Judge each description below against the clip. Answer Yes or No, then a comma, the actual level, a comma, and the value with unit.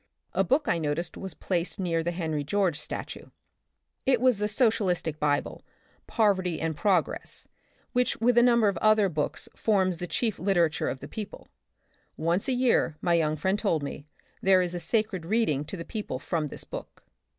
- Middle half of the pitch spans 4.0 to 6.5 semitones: Yes, average, 4.8 semitones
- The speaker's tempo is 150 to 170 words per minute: No, average, 190 wpm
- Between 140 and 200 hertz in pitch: Yes, medium, 185 Hz